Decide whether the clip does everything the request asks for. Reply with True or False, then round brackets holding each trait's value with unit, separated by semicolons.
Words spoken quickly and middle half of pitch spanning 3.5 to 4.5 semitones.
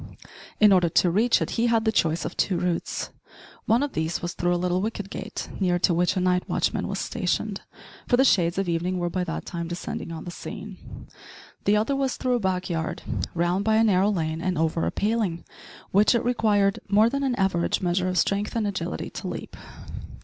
True (215 wpm; 3.8 semitones)